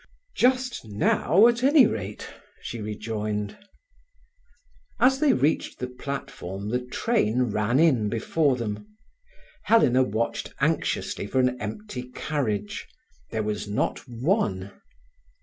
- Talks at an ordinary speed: No, slow, 115 wpm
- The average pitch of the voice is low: Yes, low, 125 Hz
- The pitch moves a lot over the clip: Yes, wide, 8.9 semitones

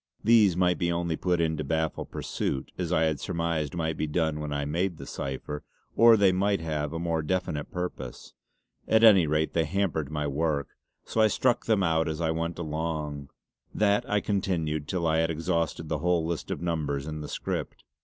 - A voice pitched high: No, very low, 80 Hz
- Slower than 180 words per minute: No, average, 200 wpm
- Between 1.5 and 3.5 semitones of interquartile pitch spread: Yes, average, 2.7 semitones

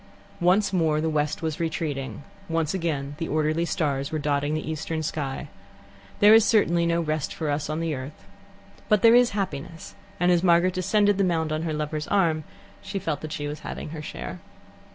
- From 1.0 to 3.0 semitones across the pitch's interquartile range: Yes, average, 2.7 semitones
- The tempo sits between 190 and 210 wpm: Yes, average, 195 wpm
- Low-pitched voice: No, medium, 160 Hz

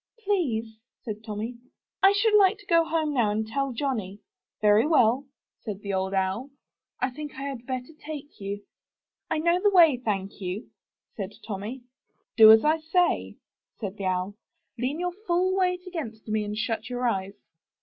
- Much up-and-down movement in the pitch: Yes, wide, 7.1 semitones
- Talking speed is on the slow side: No, average, 170 wpm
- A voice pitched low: No, high, 245 Hz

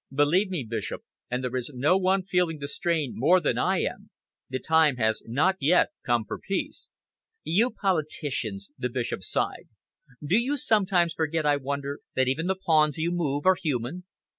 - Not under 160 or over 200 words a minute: Yes, average, 175 wpm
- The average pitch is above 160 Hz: No, medium, 155 Hz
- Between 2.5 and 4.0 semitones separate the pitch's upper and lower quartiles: No, wide, 5.5 semitones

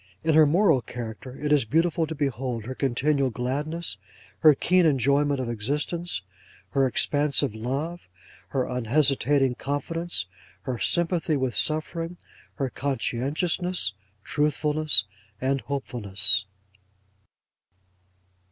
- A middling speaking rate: No, slow, 105 wpm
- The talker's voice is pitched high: No, medium, 140 Hz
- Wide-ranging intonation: No, average, 3.8 semitones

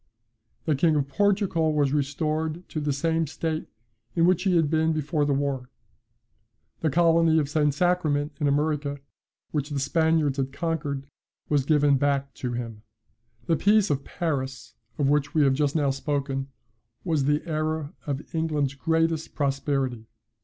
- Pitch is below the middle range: No, medium, 150 Hz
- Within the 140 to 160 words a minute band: Yes, average, 155 wpm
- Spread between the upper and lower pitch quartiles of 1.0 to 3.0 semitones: Yes, narrow, 2.5 semitones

